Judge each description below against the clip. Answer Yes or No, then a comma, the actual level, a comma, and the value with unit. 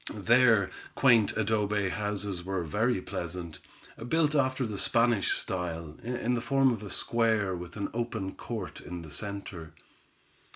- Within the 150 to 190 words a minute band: No, average, 140 wpm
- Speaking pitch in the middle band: No, low, 105 Hz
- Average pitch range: Yes, average, 4.1 semitones